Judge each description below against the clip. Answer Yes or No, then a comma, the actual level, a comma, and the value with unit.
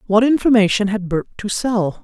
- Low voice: No, high, 210 Hz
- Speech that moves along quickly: No, average, 175 wpm